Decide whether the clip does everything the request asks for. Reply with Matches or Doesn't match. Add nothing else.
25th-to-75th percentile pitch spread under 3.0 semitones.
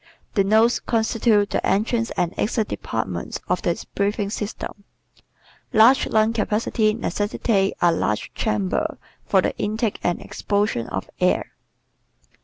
Matches